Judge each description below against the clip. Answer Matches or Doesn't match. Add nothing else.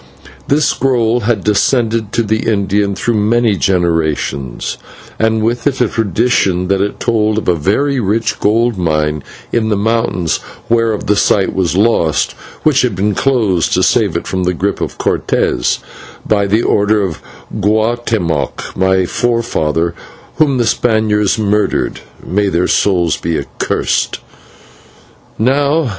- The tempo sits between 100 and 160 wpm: Matches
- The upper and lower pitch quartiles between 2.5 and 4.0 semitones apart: Matches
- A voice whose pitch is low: Matches